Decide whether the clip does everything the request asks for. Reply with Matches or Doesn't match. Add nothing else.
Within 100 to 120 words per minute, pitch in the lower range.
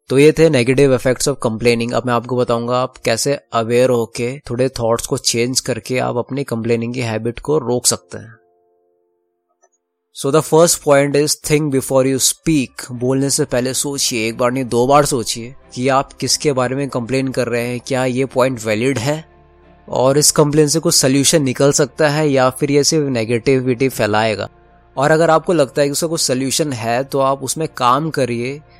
Doesn't match